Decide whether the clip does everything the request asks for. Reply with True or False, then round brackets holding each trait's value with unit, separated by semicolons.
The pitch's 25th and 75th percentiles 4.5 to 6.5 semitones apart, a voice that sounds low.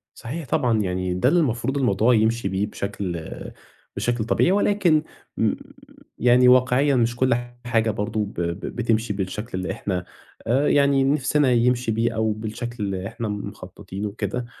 False (3.7 semitones; 115 Hz)